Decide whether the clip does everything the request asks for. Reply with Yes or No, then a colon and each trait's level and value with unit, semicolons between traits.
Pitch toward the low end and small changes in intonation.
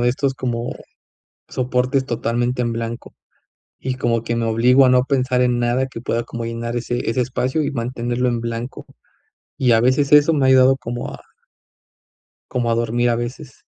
Yes: low, 120 Hz; narrow, 1.7 semitones